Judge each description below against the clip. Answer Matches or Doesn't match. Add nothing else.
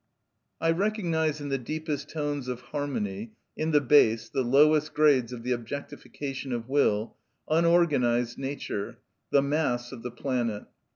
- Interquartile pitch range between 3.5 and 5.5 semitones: Matches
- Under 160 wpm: Matches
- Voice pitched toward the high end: Doesn't match